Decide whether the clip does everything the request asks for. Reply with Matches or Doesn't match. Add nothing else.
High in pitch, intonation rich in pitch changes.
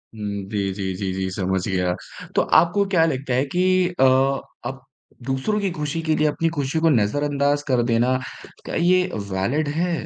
Doesn't match